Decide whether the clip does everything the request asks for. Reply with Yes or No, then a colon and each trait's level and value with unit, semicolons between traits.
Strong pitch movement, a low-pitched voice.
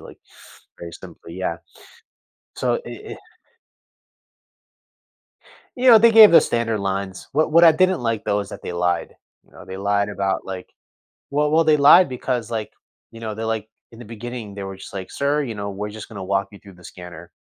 Yes: wide, 6.3 semitones; low, 110 Hz